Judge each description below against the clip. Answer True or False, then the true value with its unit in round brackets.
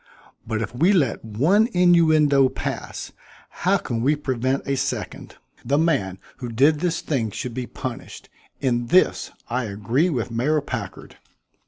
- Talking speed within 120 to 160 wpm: True (150 wpm)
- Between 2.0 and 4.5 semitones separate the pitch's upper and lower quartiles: False (4.9 semitones)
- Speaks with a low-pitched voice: True (130 Hz)